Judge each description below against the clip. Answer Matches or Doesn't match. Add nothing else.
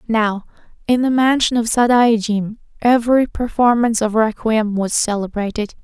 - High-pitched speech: Matches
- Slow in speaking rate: Matches